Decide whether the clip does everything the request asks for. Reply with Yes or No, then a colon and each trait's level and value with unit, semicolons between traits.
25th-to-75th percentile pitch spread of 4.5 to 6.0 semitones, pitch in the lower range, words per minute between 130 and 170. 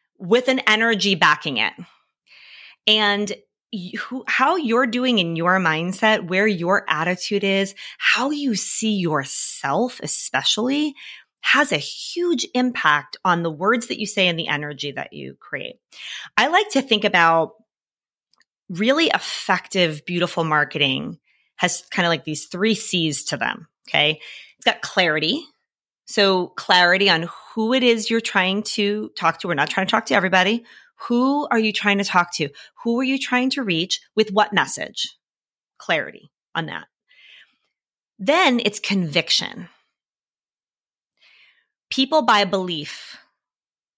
No: average, 4.9 semitones; high, 200 Hz; average, 140 wpm